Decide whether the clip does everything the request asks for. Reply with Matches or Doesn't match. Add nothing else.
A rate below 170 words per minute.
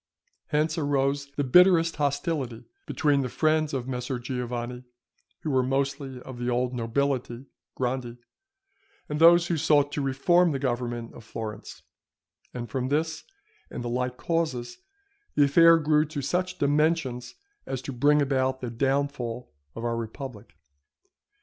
Matches